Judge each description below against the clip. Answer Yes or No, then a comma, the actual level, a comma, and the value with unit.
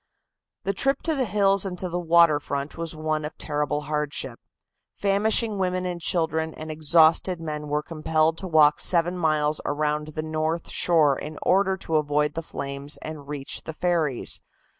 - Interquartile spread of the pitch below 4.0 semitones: Yes, average, 2.9 semitones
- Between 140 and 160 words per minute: No, average, 170 wpm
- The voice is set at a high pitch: No, medium, 160 Hz